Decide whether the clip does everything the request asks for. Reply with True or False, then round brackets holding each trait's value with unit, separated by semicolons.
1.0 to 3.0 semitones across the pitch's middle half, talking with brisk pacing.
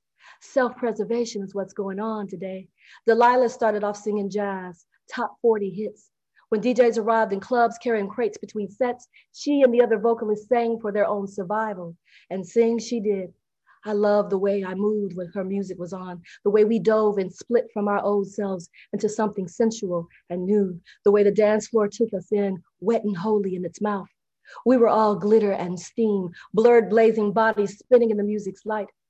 False (2.5 semitones; 190 wpm)